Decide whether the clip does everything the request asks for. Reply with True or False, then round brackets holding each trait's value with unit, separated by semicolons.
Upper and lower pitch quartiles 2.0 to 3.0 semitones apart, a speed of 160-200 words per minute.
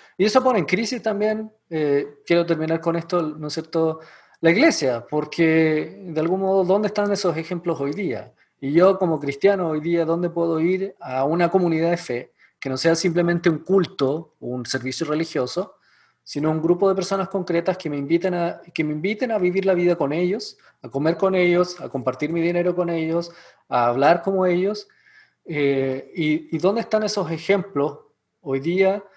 False (3.6 semitones; 185 wpm)